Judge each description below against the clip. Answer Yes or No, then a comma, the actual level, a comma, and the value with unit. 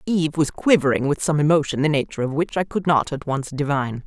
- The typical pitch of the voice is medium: Yes, medium, 150 Hz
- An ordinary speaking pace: No, fast, 235 wpm